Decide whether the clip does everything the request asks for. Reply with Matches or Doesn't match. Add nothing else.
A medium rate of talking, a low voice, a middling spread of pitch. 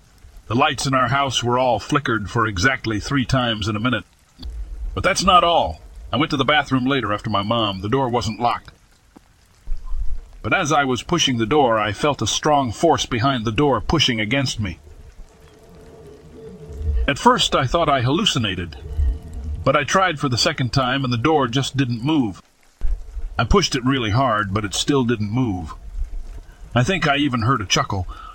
Doesn't match